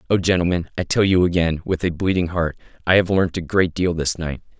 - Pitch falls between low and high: No, very low, 85 Hz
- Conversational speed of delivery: No, fast, 235 wpm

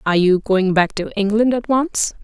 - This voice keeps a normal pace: No, fast, 215 wpm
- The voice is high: Yes, high, 210 Hz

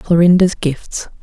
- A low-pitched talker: No, medium, 170 Hz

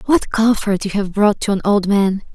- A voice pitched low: No, high, 205 Hz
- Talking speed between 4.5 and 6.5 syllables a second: Yes, 4.8 syllables/s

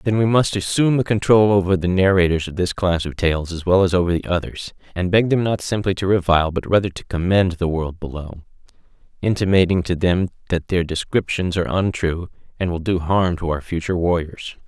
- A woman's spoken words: No, male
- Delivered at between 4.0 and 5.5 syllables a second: No, 5.7 syllables/s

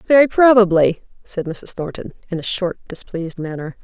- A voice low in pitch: No, high, 190 Hz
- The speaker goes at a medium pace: Yes, average, 155 wpm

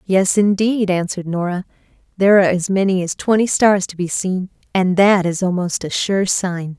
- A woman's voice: Yes, female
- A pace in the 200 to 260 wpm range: No, average, 185 wpm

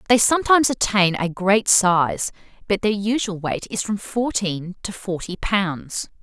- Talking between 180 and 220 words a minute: No, average, 155 wpm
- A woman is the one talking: Yes, female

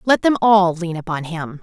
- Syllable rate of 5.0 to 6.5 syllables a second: No, 4.6 syllables/s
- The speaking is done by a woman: Yes, female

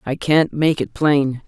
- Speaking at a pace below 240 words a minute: Yes, fast, 205 wpm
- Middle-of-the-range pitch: Yes, medium, 145 Hz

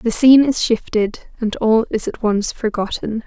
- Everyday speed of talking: Yes, average, 185 wpm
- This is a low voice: No, high, 225 Hz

